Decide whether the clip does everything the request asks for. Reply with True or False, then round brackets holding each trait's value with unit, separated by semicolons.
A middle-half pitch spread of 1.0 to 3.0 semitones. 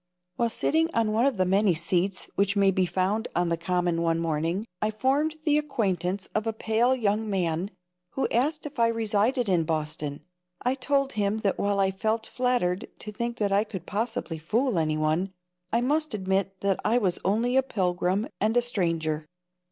False (4.8 semitones)